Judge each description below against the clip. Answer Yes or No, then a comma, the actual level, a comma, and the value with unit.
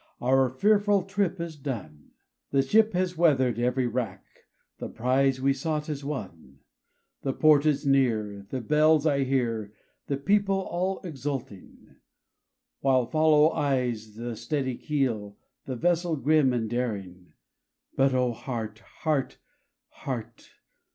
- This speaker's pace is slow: Yes, slow, 130 wpm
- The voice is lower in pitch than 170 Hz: Yes, low, 135 Hz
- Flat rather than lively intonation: No, average, 4.6 semitones